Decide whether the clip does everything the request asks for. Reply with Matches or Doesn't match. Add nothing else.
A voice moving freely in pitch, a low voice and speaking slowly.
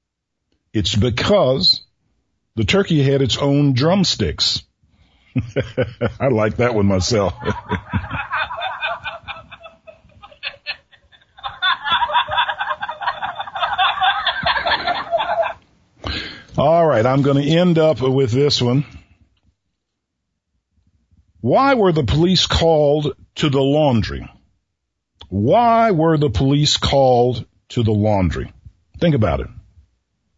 Matches